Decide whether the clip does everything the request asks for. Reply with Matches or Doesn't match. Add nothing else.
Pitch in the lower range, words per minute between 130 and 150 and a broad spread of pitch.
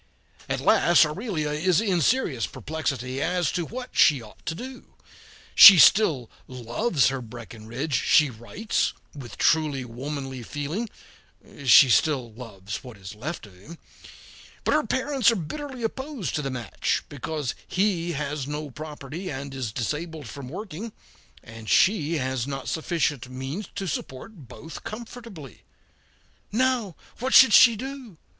Doesn't match